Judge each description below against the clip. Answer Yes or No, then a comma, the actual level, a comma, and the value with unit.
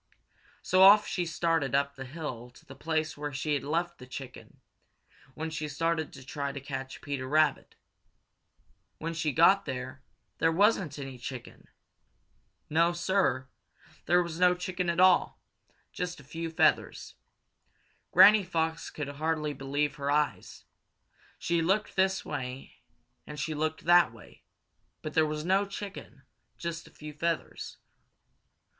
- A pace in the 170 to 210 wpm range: No, average, 150 wpm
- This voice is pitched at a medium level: Yes, medium, 155 Hz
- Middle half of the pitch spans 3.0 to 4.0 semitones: Yes, average, 3.5 semitones